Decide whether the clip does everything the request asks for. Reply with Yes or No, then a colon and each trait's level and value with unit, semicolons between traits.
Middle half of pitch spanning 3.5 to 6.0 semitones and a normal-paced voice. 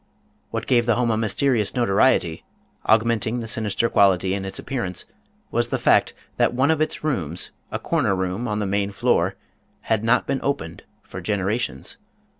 Yes: average, 3.8 semitones; average, 170 wpm